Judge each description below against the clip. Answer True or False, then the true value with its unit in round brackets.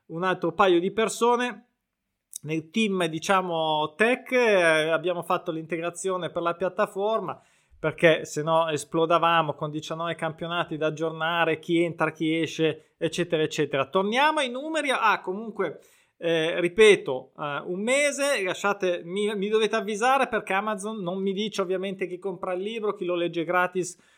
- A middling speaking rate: True (150 wpm)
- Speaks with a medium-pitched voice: True (180 Hz)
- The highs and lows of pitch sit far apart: False (4.5 semitones)